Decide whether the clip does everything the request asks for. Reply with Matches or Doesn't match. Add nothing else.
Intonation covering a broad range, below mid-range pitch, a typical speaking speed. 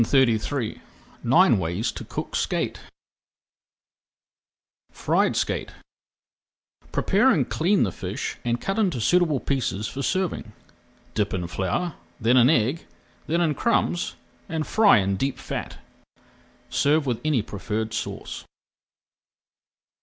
Doesn't match